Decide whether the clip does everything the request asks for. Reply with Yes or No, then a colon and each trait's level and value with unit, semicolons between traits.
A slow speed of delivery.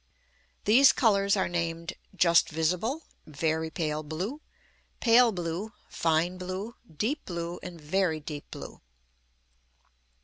Yes: slow, 110 wpm